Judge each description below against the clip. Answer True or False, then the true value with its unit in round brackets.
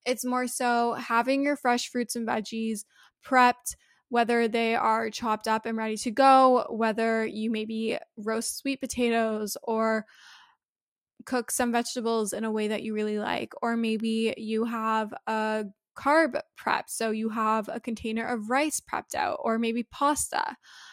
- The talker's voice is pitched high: True (230 Hz)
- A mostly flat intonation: True (1.8 semitones)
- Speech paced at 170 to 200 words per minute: False (160 wpm)